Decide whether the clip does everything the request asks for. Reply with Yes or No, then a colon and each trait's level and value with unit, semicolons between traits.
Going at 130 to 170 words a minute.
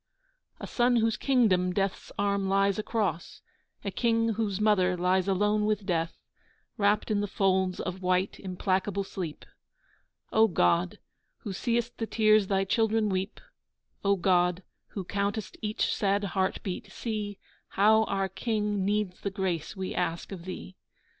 Yes: average, 145 wpm